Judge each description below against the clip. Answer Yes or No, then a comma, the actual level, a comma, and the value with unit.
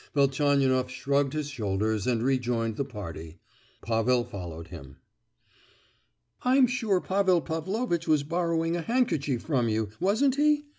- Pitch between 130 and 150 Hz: Yes, medium, 140 Hz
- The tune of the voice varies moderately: No, wide, 7.6 semitones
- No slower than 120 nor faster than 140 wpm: Yes, slow, 135 wpm